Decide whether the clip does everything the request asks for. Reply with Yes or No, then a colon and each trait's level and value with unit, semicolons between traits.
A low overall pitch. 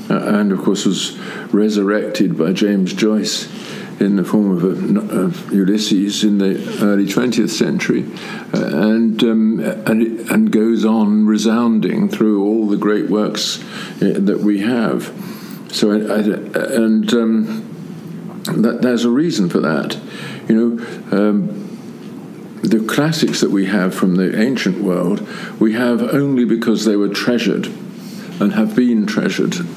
Yes: low, 110 Hz